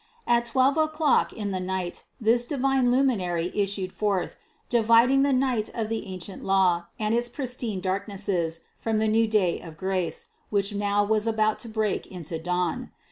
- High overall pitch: Yes, high, 215 Hz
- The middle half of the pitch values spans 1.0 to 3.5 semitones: No, average, 4.2 semitones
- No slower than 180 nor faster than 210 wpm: No, average, 165 wpm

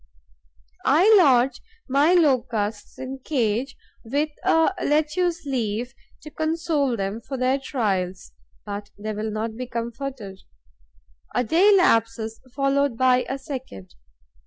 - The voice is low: No, very high, 255 Hz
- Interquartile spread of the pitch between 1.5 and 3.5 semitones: No, average, 4.6 semitones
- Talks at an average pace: No, slow, 120 wpm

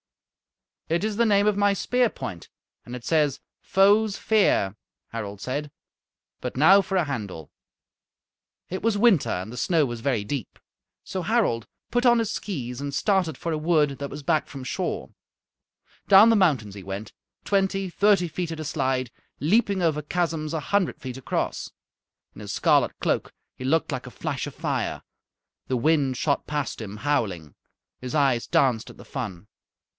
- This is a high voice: No, medium, 150 Hz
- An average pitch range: No, wide, 7.4 semitones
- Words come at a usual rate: Yes, average, 170 wpm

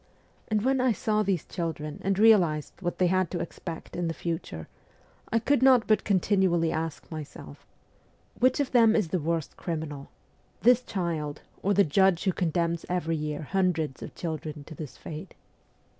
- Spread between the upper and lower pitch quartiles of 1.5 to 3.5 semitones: No, average, 4.2 semitones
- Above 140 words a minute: Yes, average, 175 wpm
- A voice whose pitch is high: No, medium, 175 Hz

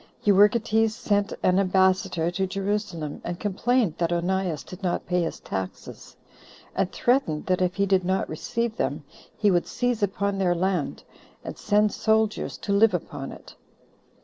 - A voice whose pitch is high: Yes, high, 195 Hz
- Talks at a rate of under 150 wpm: No, average, 155 wpm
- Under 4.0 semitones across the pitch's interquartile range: Yes, average, 2.8 semitones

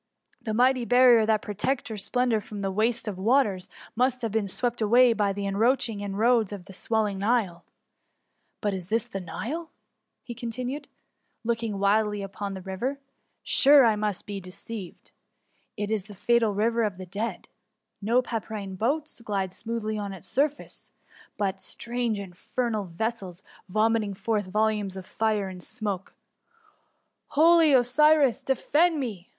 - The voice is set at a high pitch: Yes, high, 220 Hz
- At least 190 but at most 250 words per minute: No, average, 155 wpm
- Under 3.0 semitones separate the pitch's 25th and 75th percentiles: No, average, 3.4 semitones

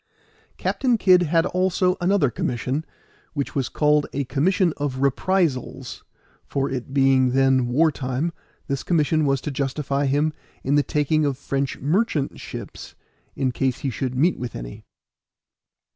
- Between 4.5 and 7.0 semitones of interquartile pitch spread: No, average, 3.4 semitones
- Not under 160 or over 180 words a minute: No, average, 145 wpm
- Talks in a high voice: No, medium, 140 Hz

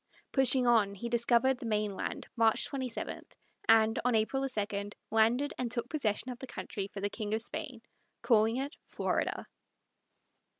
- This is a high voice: Yes, high, 230 Hz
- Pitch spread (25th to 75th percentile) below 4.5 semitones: Yes, average, 2.9 semitones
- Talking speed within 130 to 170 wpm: Yes, average, 155 wpm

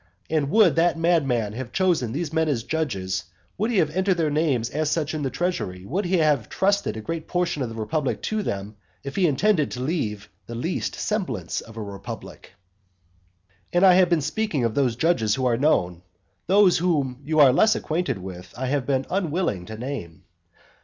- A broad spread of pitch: Yes, wide, 7.1 semitones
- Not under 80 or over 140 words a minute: No, average, 200 wpm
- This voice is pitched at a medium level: Yes, medium, 145 Hz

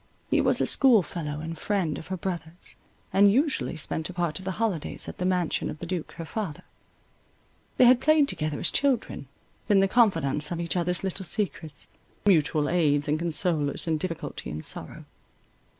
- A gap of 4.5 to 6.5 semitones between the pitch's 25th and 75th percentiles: No, average, 3.9 semitones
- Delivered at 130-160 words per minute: No, average, 180 wpm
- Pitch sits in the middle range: Yes, medium, 175 Hz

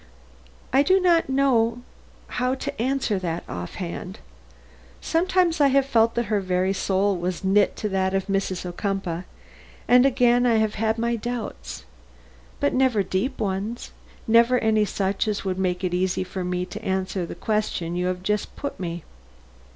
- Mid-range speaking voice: No, high, 210 Hz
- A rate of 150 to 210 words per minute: Yes, average, 165 wpm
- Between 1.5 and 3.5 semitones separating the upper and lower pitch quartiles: No, average, 4.7 semitones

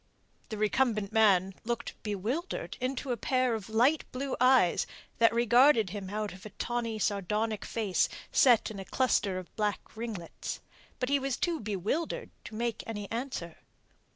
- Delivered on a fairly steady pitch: No, average, 3.6 semitones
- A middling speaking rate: Yes, average, 160 wpm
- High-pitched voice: Yes, high, 225 Hz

